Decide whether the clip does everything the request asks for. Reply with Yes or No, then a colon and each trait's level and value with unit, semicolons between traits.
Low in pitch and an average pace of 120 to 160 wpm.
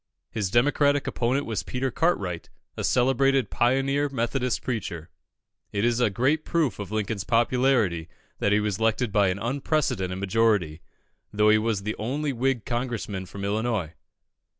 Yes: low, 115 Hz; average, 150 wpm